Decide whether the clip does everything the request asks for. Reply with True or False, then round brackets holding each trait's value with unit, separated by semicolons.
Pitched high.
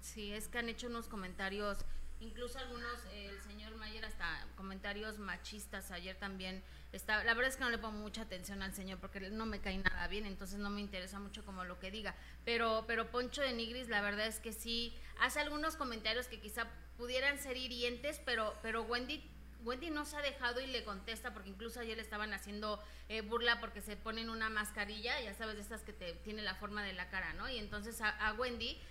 True (220 Hz)